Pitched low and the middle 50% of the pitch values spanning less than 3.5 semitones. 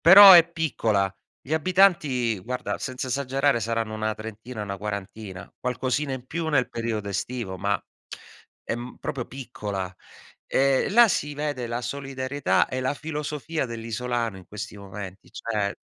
No: low, 125 Hz; average, 4.8 semitones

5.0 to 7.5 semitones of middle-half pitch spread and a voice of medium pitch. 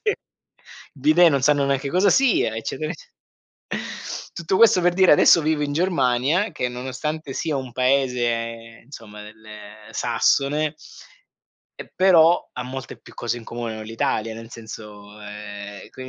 No: average, 5.3 semitones; low, 130 Hz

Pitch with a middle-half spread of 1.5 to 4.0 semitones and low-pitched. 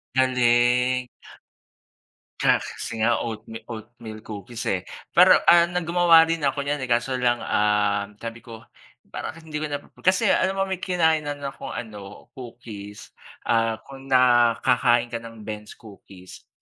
No: average, 4.4 semitones; low, 120 Hz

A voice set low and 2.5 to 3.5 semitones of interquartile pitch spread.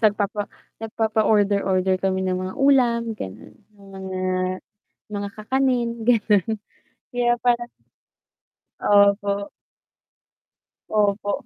No: high, 210 Hz; average, 2.8 semitones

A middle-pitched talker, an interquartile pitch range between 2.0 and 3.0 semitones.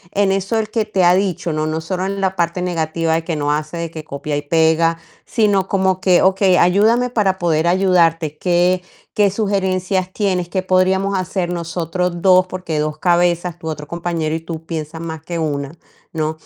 Yes: medium, 175 Hz; average, 2.7 semitones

